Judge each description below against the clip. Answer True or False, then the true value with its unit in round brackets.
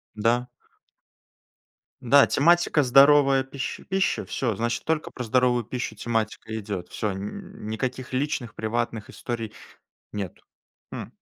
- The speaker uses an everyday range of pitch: True (3.7 semitones)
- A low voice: True (120 Hz)